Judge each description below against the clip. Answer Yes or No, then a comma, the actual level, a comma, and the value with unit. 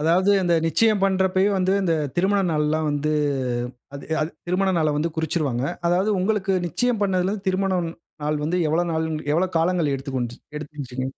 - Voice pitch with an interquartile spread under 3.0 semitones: No, average, 3.8 semitones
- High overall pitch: No, medium, 170 Hz